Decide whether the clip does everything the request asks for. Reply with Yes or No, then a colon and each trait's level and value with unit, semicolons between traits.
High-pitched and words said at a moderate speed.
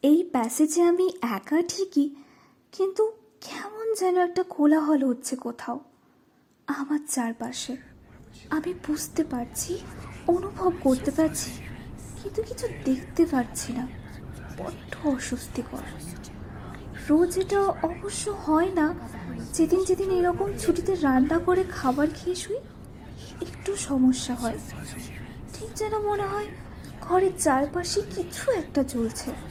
Yes: very high, 325 Hz; average, 110 wpm